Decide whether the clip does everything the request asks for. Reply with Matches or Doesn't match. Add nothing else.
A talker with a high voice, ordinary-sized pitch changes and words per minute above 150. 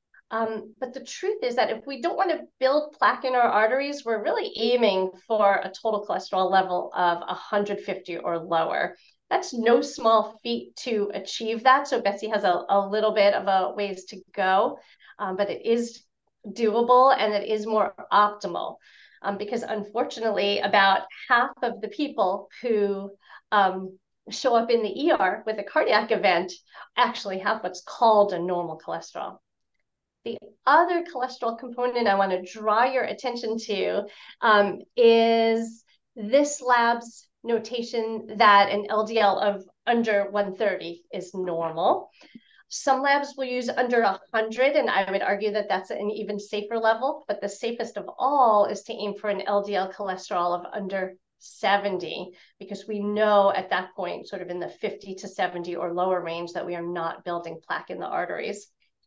Matches